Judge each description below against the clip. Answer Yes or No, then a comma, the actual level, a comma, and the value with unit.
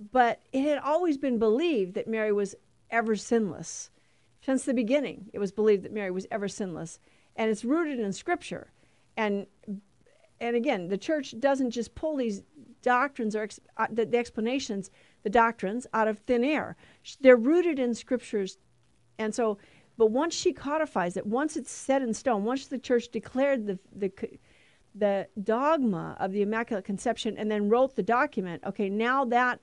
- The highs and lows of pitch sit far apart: No, average, 4.0 semitones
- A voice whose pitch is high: Yes, high, 230 Hz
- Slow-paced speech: No, average, 170 wpm